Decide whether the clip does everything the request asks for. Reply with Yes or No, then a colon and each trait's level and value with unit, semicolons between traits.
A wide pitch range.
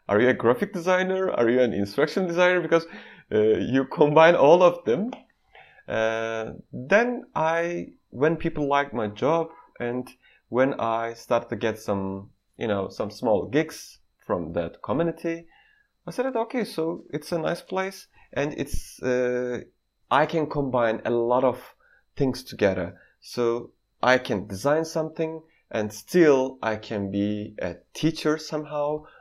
Yes: wide, 5.9 semitones